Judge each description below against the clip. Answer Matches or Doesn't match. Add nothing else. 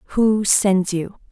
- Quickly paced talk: Doesn't match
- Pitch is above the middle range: Matches